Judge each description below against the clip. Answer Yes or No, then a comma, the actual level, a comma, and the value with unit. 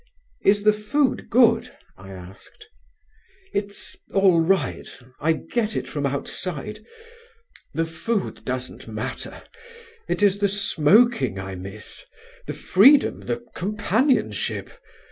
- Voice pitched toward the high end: Yes, high, 195 Hz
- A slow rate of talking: Yes, slow, 110 wpm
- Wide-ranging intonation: Yes, wide, 7.5 semitones